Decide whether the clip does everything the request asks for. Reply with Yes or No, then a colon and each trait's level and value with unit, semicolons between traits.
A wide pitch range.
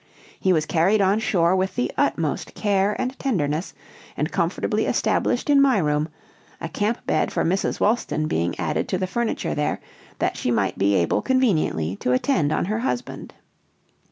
Yes: wide, 6.6 semitones